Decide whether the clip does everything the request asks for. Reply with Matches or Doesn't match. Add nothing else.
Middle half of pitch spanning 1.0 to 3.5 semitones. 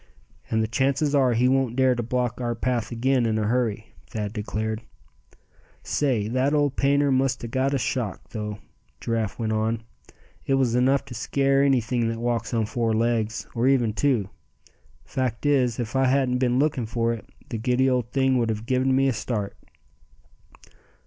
Matches